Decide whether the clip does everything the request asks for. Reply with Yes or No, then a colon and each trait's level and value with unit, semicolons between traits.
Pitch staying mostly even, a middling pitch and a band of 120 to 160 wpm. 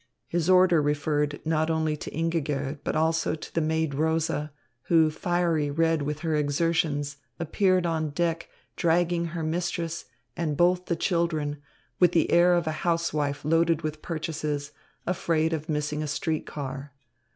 Yes: narrow, 2.1 semitones; medium, 160 Hz; average, 150 wpm